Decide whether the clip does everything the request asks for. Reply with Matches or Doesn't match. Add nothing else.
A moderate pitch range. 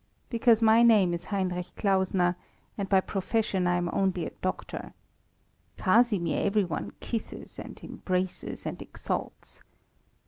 Matches